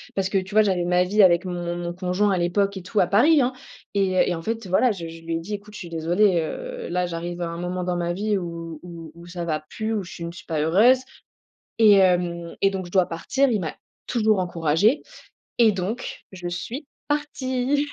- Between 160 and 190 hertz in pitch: Yes, medium, 185 Hz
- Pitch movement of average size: Yes, average, 3.5 semitones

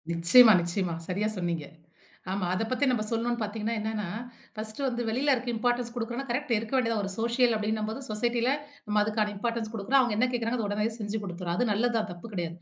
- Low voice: No, high, 220 Hz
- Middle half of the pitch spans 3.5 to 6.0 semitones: No, narrow, 2.6 semitones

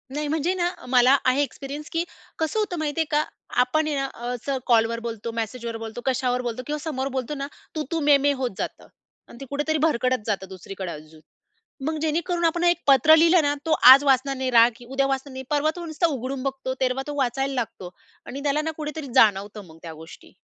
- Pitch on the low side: No, very high, 270 Hz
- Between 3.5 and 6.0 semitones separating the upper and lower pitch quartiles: Yes, average, 4.1 semitones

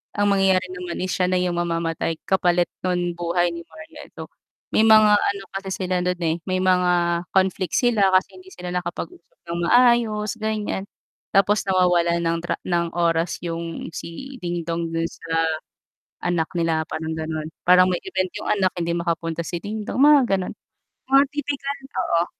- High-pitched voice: No, medium, 180 Hz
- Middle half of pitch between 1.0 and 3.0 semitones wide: Yes, average, 2.7 semitones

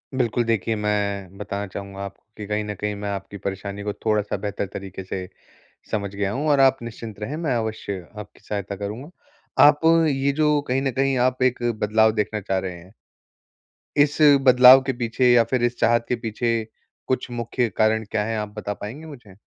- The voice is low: Yes, low, 110 Hz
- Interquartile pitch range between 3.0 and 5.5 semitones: Yes, average, 3.7 semitones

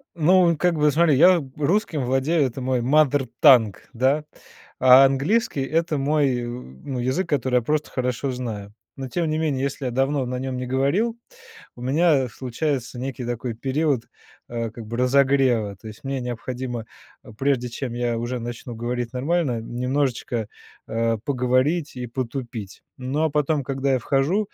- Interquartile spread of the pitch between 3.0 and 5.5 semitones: Yes, average, 3.3 semitones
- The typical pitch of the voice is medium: No, low, 130 Hz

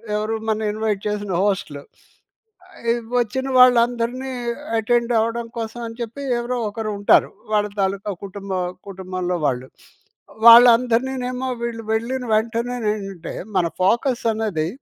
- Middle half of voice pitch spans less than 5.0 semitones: Yes, average, 3.0 semitones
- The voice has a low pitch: No, high, 225 Hz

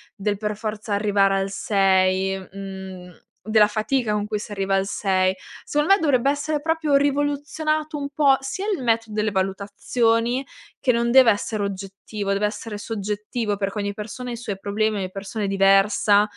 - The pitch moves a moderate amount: Yes, average, 4.2 semitones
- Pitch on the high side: Yes, high, 210 Hz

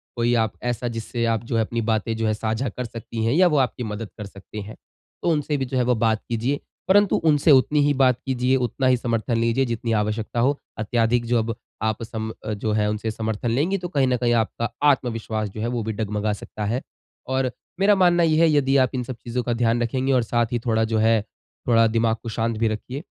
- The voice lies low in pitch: Yes, low, 115 Hz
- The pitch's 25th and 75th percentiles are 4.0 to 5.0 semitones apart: No, average, 2.8 semitones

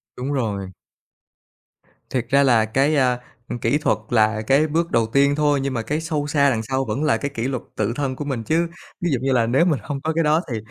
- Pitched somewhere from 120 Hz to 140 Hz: Yes, low, 135 Hz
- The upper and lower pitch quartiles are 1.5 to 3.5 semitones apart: No, average, 3.9 semitones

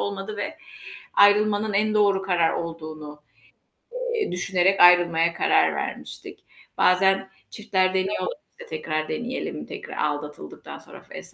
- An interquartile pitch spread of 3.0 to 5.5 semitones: Yes, average, 3.5 semitones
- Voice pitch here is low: No, high, 190 Hz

